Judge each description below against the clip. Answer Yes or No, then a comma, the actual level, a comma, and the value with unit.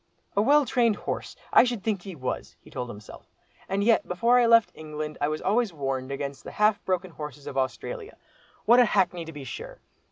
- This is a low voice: No, medium, 185 Hz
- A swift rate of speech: Yes, fast, 215 wpm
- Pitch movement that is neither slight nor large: No, wide, 7.9 semitones